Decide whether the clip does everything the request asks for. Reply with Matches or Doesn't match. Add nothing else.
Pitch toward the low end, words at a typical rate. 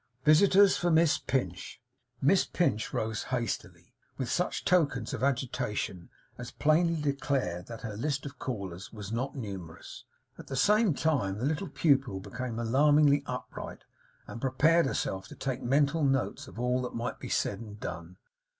Matches